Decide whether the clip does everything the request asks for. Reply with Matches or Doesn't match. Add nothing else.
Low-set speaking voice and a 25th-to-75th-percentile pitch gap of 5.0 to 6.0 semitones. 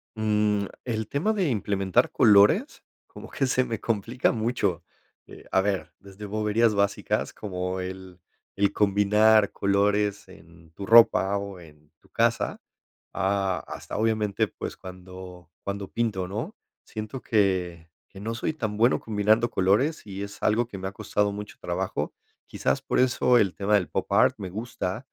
Doesn't match